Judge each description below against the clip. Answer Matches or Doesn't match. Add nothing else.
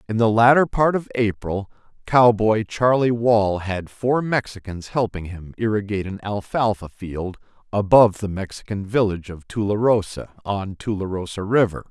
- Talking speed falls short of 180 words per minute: Matches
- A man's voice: Matches